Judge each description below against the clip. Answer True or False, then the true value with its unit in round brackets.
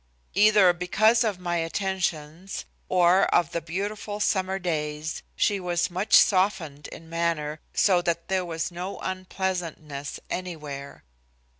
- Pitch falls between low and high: True (180 Hz)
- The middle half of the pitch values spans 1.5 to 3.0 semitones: True (2.7 semitones)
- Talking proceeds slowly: True (125 wpm)